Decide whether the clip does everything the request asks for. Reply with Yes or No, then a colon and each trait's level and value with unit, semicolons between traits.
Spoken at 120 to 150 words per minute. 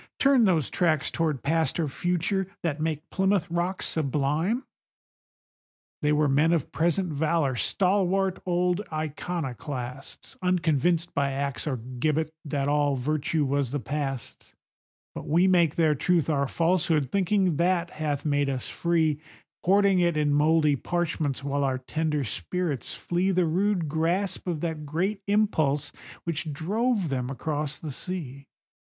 Yes: average, 140 wpm